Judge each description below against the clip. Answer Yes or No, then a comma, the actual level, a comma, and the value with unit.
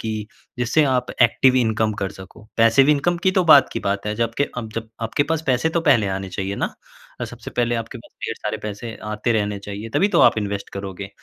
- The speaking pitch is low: Yes, low, 115 Hz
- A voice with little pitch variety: No, average, 3.8 semitones